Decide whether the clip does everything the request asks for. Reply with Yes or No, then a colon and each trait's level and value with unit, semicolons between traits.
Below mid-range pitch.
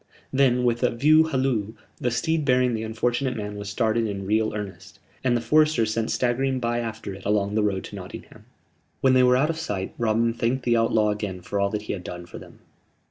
Yes: low, 115 Hz